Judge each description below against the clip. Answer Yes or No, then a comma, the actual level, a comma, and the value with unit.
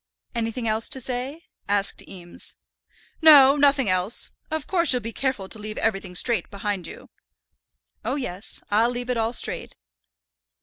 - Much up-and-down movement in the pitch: No, average, 4.5 semitones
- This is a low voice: No, high, 230 Hz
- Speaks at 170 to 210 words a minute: No, average, 155 wpm